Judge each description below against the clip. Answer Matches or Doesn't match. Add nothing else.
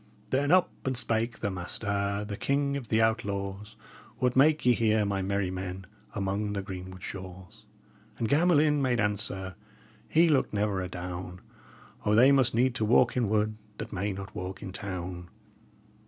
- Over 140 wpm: Matches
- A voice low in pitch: Matches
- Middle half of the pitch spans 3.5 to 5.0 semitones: Matches